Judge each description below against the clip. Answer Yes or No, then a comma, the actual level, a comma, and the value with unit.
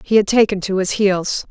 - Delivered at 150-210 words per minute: No, fast, 240 wpm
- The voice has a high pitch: Yes, high, 200 Hz